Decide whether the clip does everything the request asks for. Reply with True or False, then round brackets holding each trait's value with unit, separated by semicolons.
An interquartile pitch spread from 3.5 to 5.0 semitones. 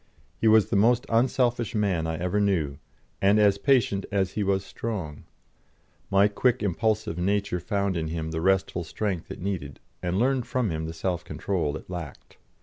True (4.0 semitones)